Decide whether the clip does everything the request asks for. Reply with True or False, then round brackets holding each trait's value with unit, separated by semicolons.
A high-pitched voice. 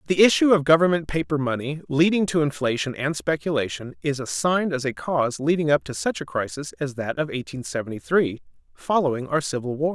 False (145 Hz)